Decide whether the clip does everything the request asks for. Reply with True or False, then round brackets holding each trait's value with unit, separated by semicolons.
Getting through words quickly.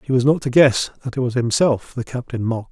True (265 wpm)